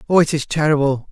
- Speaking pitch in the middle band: Yes, medium, 150 Hz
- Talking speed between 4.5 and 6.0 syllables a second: No, 6.5 syllables/s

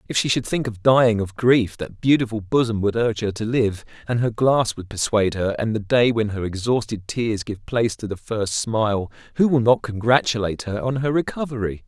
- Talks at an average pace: No, fast, 215 wpm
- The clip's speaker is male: Yes, male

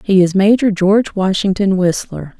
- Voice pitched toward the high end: Yes, high, 195 Hz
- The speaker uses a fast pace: No, average, 150 wpm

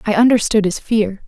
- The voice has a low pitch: No, high, 215 Hz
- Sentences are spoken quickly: No, average, 190 wpm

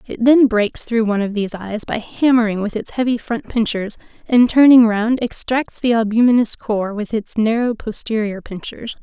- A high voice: Yes, high, 225 Hz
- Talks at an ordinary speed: Yes, average, 180 wpm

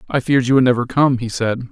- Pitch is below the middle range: Yes, low, 125 Hz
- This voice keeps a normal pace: No, fast, 280 wpm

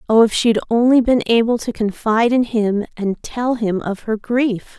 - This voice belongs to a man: No, female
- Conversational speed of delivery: No, fast, 215 wpm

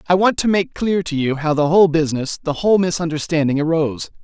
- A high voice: No, medium, 165 Hz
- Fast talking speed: Yes, fast, 215 wpm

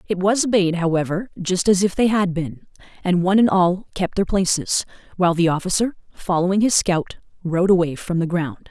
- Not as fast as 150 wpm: No, average, 195 wpm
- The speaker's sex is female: Yes, female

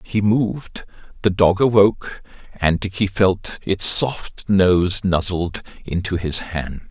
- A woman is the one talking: No, male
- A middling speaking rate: No, slow, 130 wpm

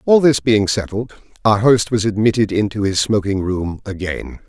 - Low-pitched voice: Yes, low, 105 Hz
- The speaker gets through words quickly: No, average, 175 wpm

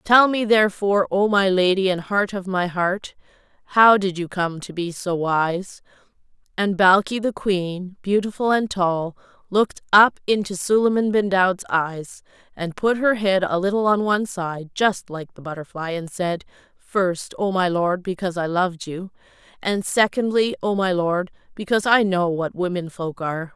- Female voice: Yes, female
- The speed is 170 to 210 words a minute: Yes, average, 175 wpm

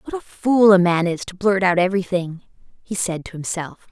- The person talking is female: Yes, female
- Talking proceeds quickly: Yes, fast, 215 wpm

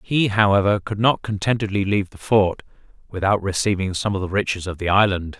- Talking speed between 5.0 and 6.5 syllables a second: Yes, 5.8 syllables/s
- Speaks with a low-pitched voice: Yes, low, 100 Hz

